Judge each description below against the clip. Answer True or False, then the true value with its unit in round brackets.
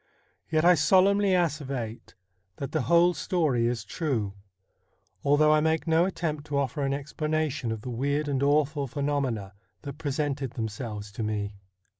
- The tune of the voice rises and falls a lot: False (4.4 semitones)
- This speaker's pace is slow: False (150 wpm)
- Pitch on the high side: False (145 Hz)